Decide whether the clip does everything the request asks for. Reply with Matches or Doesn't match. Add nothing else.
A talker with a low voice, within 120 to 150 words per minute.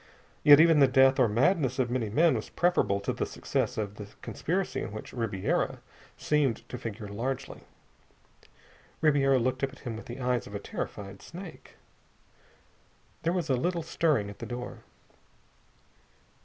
Doesn't match